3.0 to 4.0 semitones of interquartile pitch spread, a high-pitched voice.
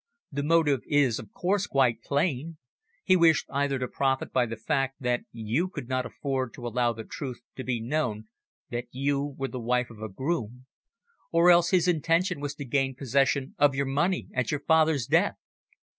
No: average, 3.7 semitones; low, 135 Hz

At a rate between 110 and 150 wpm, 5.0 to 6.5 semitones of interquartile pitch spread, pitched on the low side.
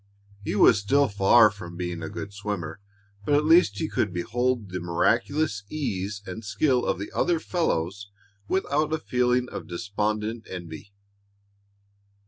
Yes: average, 145 wpm; average, 5.3 semitones; low, 105 Hz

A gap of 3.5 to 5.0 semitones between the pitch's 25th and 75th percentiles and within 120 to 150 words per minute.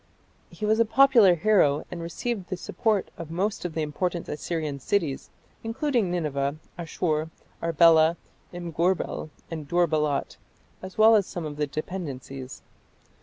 Yes: average, 4.4 semitones; average, 140 wpm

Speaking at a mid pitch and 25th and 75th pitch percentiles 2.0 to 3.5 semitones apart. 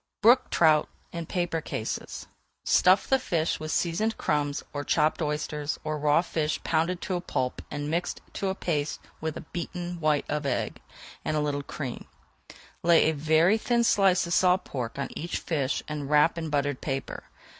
Yes: medium, 155 Hz; average, 3.0 semitones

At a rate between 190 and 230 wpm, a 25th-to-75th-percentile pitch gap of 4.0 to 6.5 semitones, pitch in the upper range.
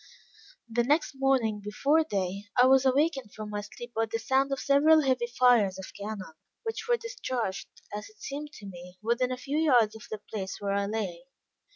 Yes: average, 195 wpm; average, 4.7 semitones; high, 240 Hz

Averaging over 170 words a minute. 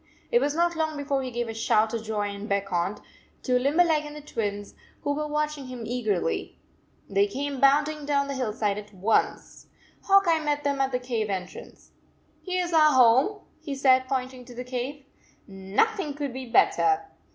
Yes: average, 190 wpm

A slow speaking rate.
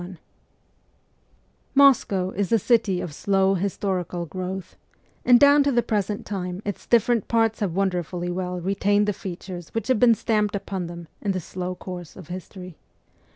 No: average, 160 wpm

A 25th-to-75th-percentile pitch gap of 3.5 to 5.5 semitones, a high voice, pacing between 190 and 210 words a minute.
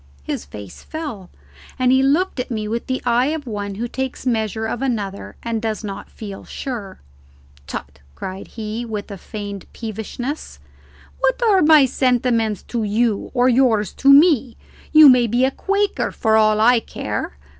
No: average, 3.8 semitones; high, 235 Hz; average, 165 wpm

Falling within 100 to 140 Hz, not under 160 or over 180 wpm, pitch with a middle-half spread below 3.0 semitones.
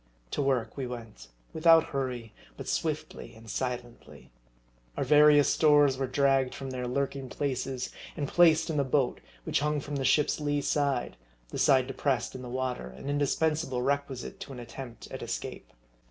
Yes: low, 135 Hz; average, 170 wpm; narrow, 2.6 semitones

